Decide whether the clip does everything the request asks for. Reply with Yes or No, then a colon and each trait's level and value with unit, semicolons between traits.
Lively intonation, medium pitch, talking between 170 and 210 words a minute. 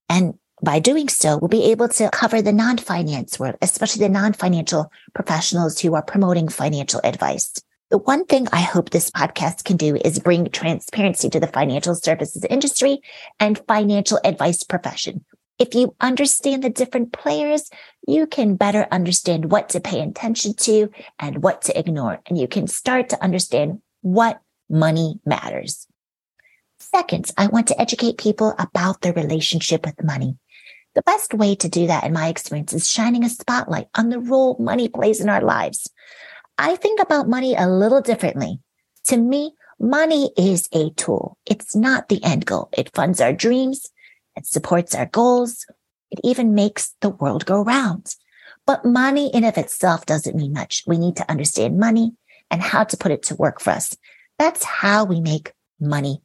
No: wide, 6.6 semitones; high, 205 Hz; average, 175 wpm